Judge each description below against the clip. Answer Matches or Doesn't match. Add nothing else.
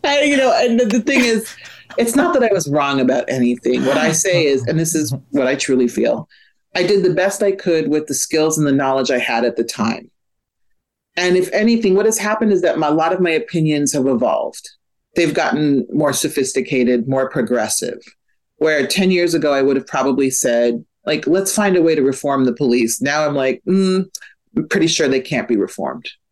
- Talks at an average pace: Doesn't match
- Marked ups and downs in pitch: Matches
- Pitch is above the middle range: Doesn't match